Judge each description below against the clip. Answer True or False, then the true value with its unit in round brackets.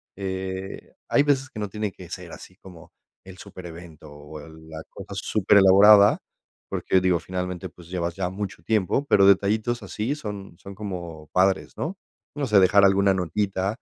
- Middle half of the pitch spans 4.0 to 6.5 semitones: False (2.6 semitones)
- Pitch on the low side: True (95 Hz)